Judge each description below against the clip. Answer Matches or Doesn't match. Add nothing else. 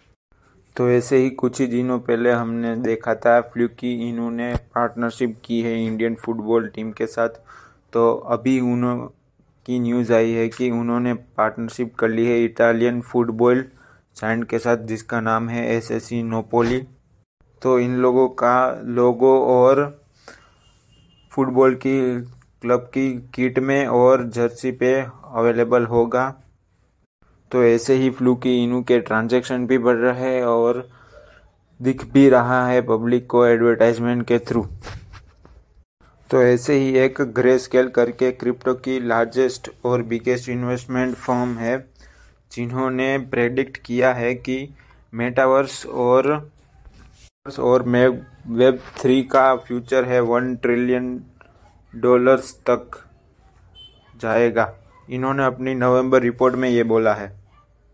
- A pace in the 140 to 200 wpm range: Doesn't match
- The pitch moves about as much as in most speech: Doesn't match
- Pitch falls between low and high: Doesn't match